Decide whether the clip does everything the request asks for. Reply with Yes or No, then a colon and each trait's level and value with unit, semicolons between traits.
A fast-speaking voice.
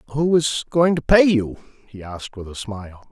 Yes: fast, 210 wpm